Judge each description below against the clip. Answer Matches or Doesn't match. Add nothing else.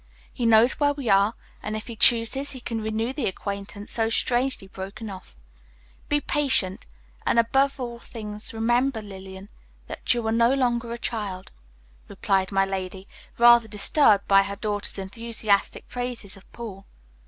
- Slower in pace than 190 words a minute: Matches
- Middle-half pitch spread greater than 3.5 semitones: Doesn't match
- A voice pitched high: Matches